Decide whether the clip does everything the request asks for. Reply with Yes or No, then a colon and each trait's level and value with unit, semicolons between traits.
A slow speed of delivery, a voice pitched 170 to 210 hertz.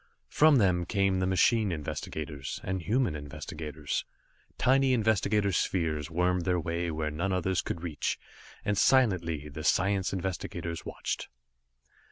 No: slow, 130 wpm; very low, 90 Hz